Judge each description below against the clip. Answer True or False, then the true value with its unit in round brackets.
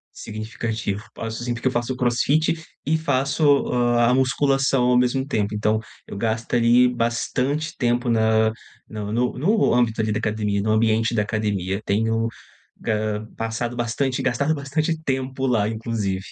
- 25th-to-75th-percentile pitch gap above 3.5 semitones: False (3.0 semitones)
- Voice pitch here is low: True (120 Hz)